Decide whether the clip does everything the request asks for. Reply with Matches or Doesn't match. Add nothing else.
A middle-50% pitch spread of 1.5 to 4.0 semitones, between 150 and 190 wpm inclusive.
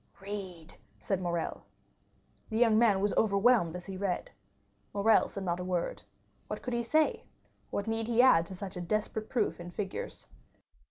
Matches